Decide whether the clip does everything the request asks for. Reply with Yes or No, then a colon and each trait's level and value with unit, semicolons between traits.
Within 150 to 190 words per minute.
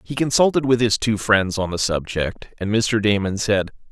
No: average, 200 wpm